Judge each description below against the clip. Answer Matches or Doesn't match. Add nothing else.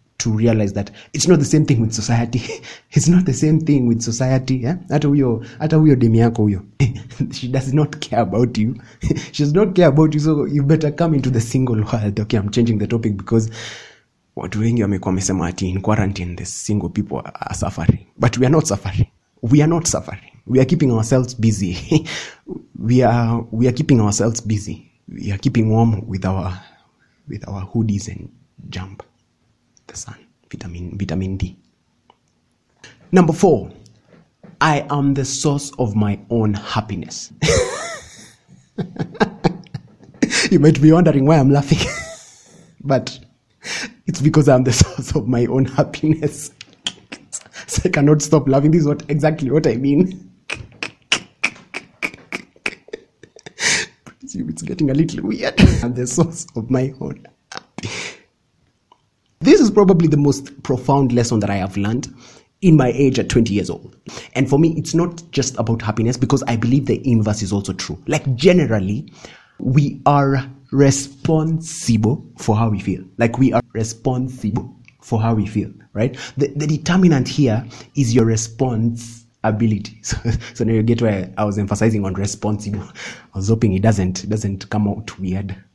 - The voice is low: Matches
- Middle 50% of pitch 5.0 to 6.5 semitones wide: Matches